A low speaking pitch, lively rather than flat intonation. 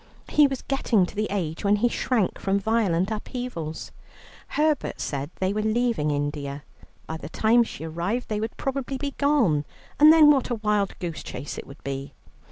No: high, 210 Hz; wide, 7.5 semitones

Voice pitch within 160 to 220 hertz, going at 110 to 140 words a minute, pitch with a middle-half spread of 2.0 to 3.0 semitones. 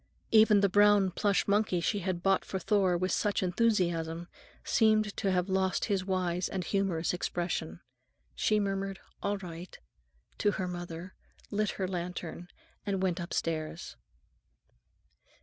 Yes: high, 190 Hz; slow, 135 wpm; narrow, 2.5 semitones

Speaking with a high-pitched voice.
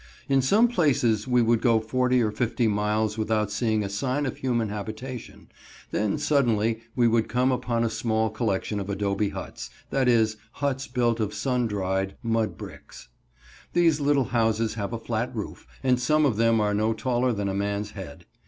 No: low, 115 Hz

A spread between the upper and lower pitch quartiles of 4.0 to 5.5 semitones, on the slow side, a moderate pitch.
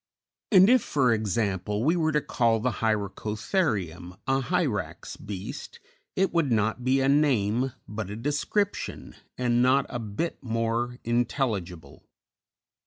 No: average, 5.2 semitones; slow, 130 wpm; low, 120 Hz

